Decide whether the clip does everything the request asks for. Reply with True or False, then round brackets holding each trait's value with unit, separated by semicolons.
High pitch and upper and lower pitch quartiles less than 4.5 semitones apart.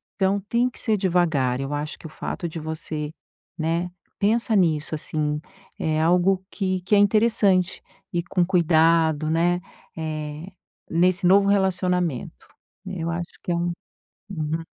False (175 Hz; 3.2 semitones)